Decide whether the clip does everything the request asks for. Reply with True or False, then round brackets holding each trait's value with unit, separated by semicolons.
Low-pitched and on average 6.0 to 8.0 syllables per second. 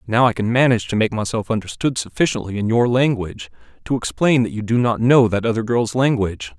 True (115 Hz; 6.1 syllables/s)